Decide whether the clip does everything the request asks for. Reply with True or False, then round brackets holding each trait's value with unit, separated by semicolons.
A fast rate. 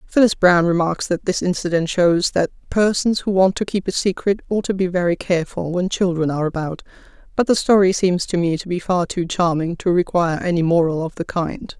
True (215 wpm)